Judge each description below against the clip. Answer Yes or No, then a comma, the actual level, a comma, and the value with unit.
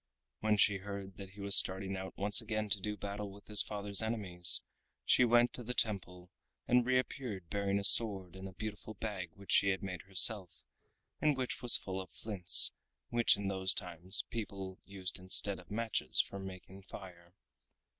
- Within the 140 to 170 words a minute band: No, average, 180 wpm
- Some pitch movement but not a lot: No, narrow, 2.2 semitones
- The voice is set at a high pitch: No, low, 100 Hz